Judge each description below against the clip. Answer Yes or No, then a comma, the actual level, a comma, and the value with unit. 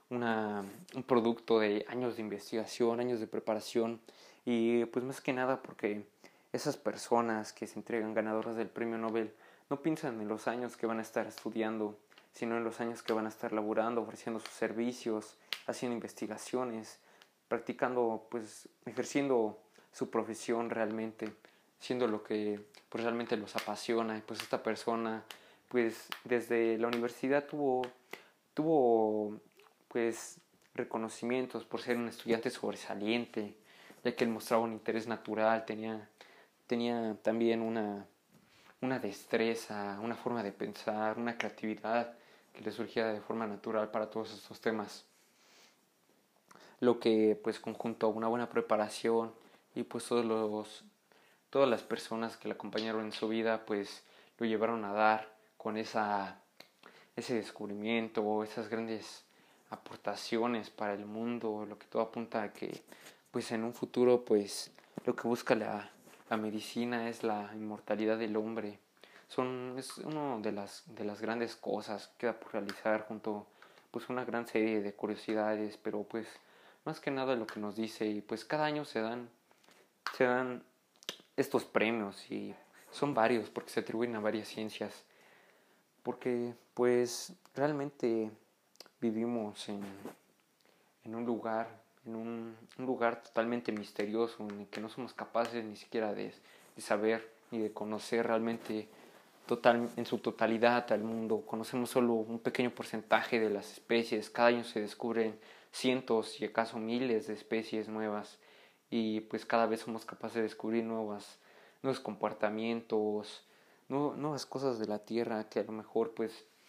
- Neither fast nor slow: Yes, average, 150 wpm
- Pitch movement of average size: No, narrow, 1.6 semitones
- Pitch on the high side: No, low, 115 Hz